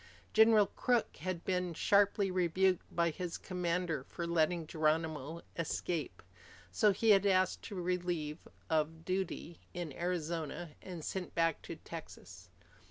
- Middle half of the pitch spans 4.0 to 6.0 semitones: No, narrow, 2.4 semitones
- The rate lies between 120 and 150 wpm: Yes, slow, 135 wpm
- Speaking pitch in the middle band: Yes, medium, 175 Hz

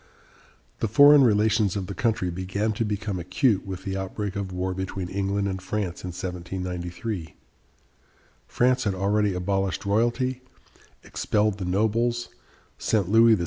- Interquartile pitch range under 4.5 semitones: Yes, average, 2.9 semitones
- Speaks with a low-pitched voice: Yes, low, 100 Hz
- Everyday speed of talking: Yes, average, 145 wpm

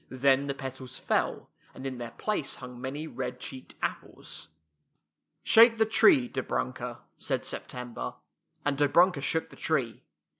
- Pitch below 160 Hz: Yes, low, 135 Hz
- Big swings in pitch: No, average, 4.3 semitones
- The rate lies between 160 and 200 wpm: No, average, 150 wpm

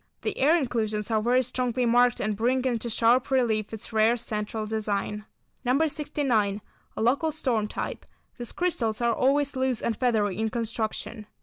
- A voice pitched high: Yes, high, 235 Hz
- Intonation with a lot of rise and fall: No, average, 3.0 semitones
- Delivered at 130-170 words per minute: Yes, average, 165 wpm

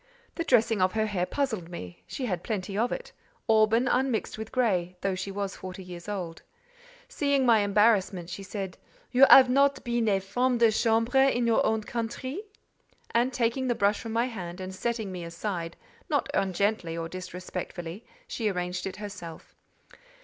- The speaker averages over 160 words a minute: Yes, average, 170 wpm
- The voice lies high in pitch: Yes, high, 210 Hz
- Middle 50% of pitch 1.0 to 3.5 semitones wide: No, average, 4.4 semitones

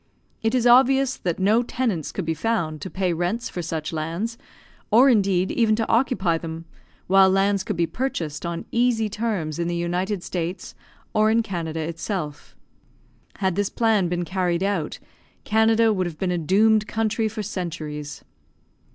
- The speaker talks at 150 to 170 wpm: Yes, average, 165 wpm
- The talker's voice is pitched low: No, high, 190 Hz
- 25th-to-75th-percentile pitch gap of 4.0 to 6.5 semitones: Yes, average, 4.6 semitones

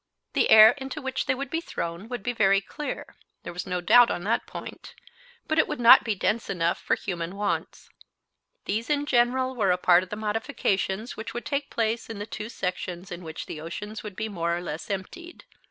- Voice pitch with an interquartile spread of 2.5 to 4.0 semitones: No, average, 5.1 semitones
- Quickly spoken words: Yes, fast, 215 wpm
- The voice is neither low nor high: No, high, 215 Hz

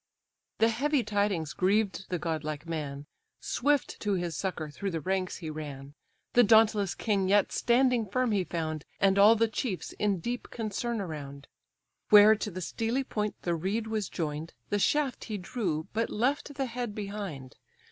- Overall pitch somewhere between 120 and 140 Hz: No, high, 200 Hz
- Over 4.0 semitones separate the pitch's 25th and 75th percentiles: Yes, average, 5.3 semitones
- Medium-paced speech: Yes, average, 165 wpm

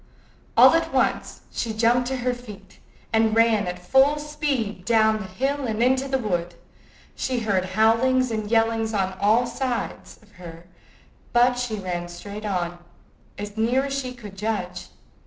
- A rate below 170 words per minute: Yes, average, 160 wpm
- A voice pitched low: No, high, 225 Hz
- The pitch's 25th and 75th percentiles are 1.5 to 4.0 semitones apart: Yes, average, 3.7 semitones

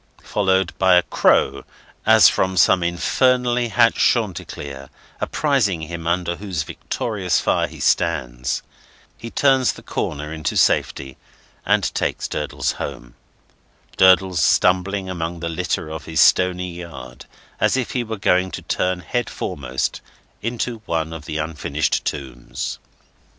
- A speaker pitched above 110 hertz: No, very low, 90 Hz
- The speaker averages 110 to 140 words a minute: Yes, slow, 135 wpm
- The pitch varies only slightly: No, average, 4.0 semitones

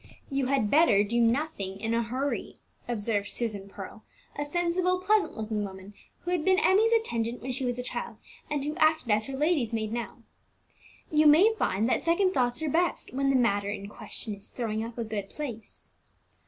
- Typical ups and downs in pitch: No, wide, 6.3 semitones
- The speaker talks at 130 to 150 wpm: No, average, 195 wpm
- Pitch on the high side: Yes, high, 245 Hz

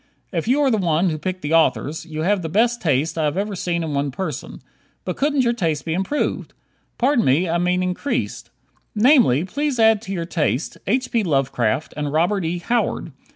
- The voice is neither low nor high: Yes, medium, 180 Hz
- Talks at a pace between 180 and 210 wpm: Yes, average, 200 wpm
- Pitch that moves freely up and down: Yes, wide, 6.0 semitones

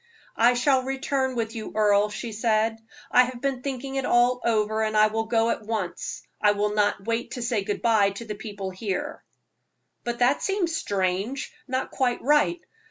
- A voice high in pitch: Yes, high, 230 Hz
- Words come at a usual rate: Yes, average, 185 wpm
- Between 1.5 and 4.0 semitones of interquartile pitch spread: Yes, average, 3.3 semitones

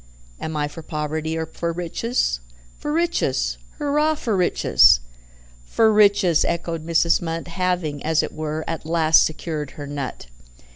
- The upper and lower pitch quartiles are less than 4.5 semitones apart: Yes, average, 3.0 semitones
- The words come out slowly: No, average, 145 wpm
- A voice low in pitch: No, medium, 165 Hz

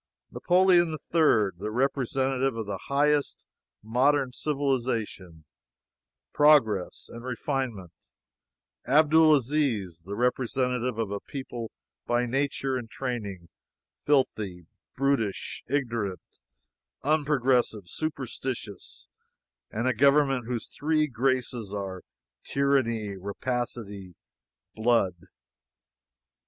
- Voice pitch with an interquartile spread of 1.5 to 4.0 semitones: No, average, 4.6 semitones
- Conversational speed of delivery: No, slow, 85 wpm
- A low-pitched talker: Yes, low, 125 Hz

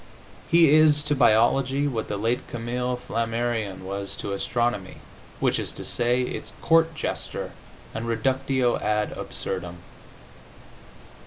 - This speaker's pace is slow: Yes, slow, 120 wpm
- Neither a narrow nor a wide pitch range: Yes, average, 3.7 semitones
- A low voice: Yes, low, 120 Hz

